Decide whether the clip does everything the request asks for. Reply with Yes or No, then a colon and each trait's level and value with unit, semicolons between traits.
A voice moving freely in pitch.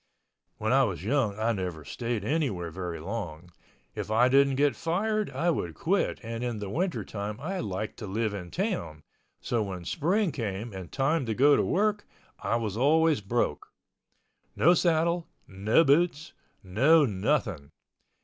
Yes: wide, 8.1 semitones